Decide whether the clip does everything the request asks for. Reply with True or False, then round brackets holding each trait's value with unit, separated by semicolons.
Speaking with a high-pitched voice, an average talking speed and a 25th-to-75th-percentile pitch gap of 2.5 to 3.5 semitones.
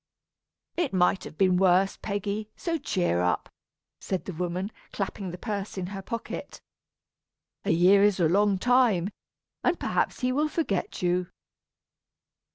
True (195 Hz; 145 wpm; 3.0 semitones)